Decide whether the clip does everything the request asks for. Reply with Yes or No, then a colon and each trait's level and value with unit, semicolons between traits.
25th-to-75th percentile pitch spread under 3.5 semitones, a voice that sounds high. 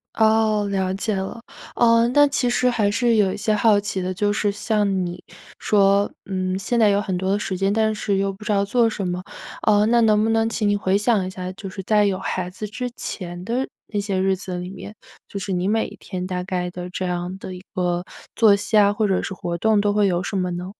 Yes: narrow, 2.5 semitones; high, 200 Hz